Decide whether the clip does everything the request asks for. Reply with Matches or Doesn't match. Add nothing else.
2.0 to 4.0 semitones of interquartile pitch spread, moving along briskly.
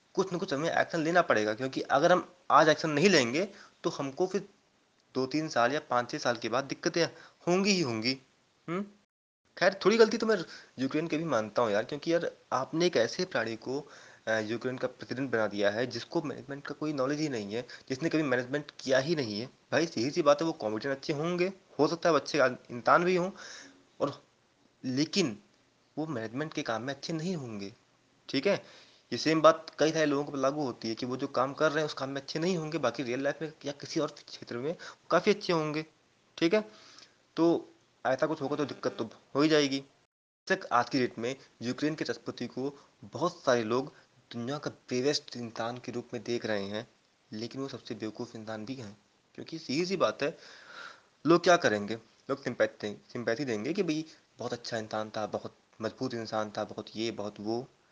Doesn't match